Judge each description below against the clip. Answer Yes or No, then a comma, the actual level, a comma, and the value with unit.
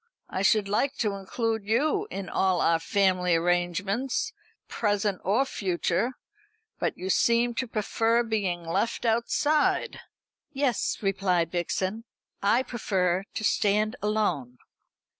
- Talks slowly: Yes, slow, 120 wpm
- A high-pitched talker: Yes, high, 205 Hz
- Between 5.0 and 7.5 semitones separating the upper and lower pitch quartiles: No, average, 4.0 semitones